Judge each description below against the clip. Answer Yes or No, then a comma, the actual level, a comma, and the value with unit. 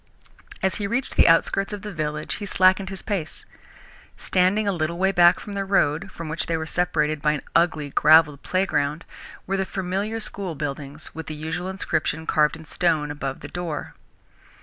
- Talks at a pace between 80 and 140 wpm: No, average, 185 wpm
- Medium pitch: Yes, medium, 170 Hz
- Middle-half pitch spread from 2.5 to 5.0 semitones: Yes, average, 3.9 semitones